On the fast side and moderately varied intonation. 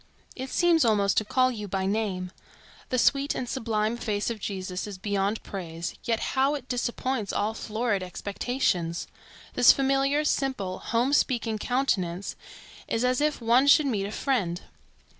No: average, 155 wpm; average, 4.8 semitones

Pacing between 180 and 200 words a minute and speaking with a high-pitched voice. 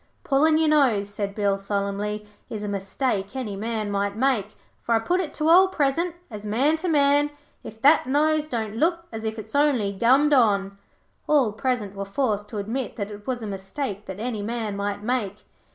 Yes: average, 195 wpm; high, 225 Hz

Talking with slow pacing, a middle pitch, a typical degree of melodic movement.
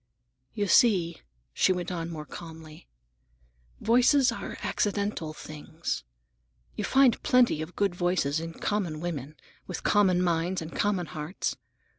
Yes: slow, 130 wpm; medium, 175 Hz; average, 4.3 semitones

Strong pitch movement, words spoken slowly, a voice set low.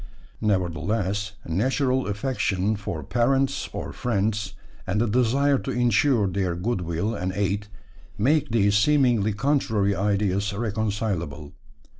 No: average, 3.8 semitones; slow, 110 wpm; low, 105 Hz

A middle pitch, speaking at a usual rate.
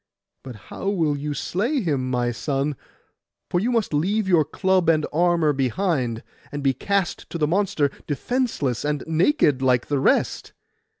Yes: medium, 155 Hz; average, 165 wpm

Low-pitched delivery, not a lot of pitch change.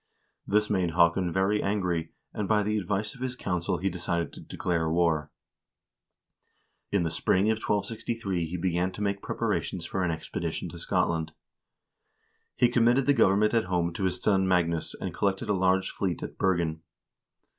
No: very low, 95 Hz; average, 3.4 semitones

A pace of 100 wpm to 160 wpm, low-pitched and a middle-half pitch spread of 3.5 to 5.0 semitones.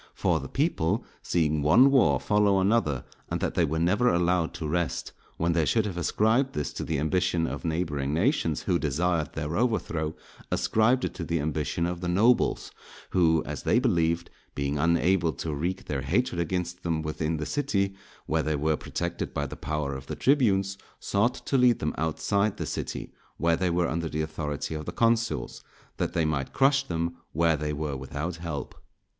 No: average, 185 wpm; very low, 85 Hz; average, 4.1 semitones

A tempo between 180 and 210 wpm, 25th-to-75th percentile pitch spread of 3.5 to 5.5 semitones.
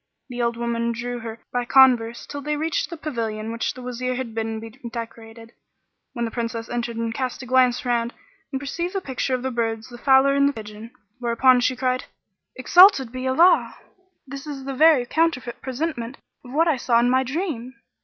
No: fast, 205 wpm; narrow, 2.6 semitones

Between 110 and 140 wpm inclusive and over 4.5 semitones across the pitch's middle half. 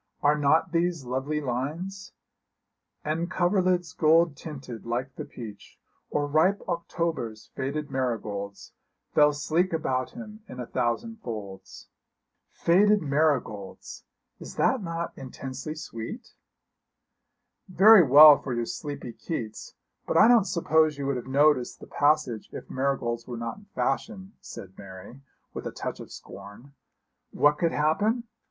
Yes: slow, 135 wpm; wide, 5.4 semitones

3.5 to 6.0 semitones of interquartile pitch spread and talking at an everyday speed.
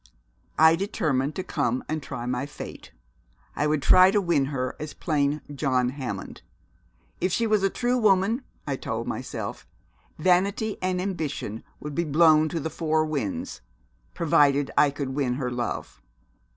Yes: average, 5.1 semitones; average, 155 wpm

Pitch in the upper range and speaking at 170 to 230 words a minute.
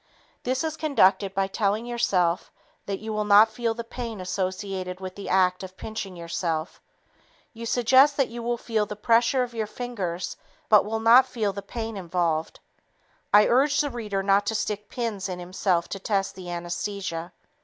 Yes: high, 205 Hz; average, 175 wpm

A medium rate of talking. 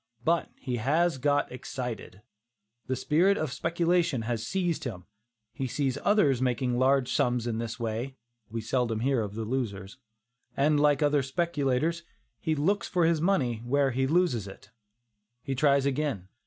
Yes: average, 155 wpm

